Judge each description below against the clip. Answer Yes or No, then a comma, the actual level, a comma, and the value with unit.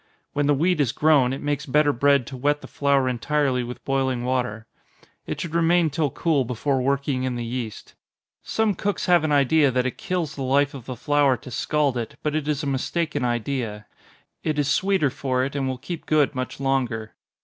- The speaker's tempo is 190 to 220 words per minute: Yes, fast, 205 wpm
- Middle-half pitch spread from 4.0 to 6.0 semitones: No, average, 2.8 semitones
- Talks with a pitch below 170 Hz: Yes, medium, 140 Hz